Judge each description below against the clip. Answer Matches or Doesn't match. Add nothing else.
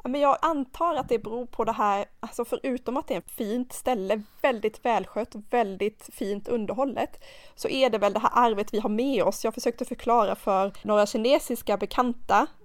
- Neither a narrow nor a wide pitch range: Matches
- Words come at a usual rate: Doesn't match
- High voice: Matches